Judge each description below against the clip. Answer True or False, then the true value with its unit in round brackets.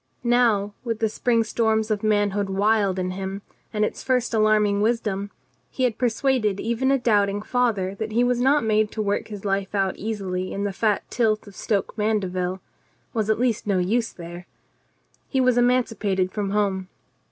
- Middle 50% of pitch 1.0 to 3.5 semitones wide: True (2.7 semitones)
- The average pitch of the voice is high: True (215 Hz)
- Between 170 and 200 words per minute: True (185 wpm)